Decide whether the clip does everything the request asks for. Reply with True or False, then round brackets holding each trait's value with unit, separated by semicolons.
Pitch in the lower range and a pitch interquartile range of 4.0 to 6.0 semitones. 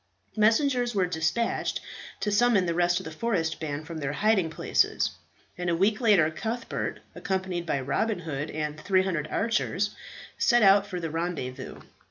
False (180 Hz; 4.9 semitones)